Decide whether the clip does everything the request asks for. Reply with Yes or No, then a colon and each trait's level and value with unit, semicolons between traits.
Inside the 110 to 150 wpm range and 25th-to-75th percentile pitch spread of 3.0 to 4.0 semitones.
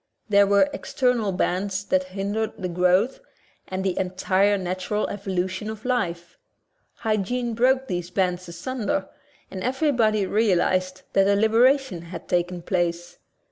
Yes: slow, 135 wpm; average, 3.3 semitones